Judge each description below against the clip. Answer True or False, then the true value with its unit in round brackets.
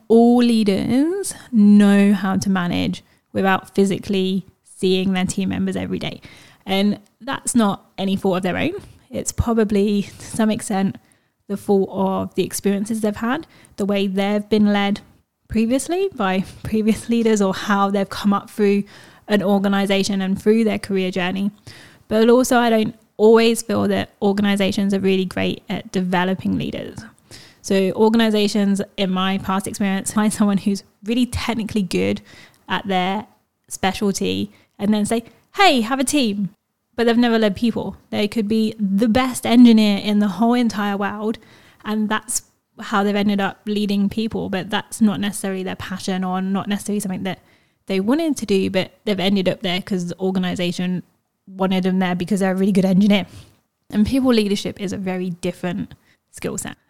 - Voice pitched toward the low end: False (200 Hz)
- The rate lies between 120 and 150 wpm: False (165 wpm)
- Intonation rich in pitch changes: False (2.5 semitones)